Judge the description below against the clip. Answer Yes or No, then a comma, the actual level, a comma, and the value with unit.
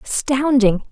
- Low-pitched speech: No, very high, 250 Hz